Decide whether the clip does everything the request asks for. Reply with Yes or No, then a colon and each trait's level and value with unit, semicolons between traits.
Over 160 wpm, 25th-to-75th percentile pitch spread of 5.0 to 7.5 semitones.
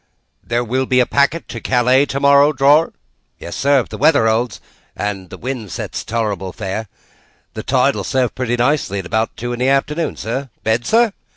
No: average, 190 wpm; average, 3.9 semitones